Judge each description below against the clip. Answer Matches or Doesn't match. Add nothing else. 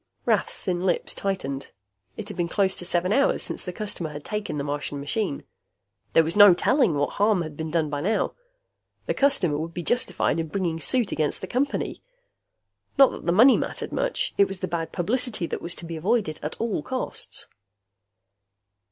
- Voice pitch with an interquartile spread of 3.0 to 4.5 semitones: Doesn't match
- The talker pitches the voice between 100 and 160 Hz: Doesn't match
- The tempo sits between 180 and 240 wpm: Matches